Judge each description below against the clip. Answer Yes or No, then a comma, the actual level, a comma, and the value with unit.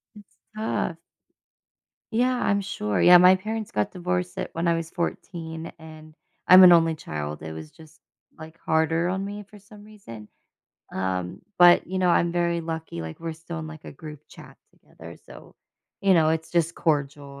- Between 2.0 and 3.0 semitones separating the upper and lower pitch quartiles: Yes, average, 2.7 semitones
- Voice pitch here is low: No, medium, 165 Hz